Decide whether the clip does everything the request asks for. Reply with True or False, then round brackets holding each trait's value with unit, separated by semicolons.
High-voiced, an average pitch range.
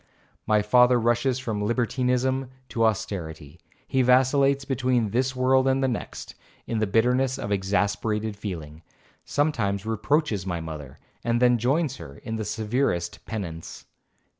False (115 Hz; 4.2 semitones)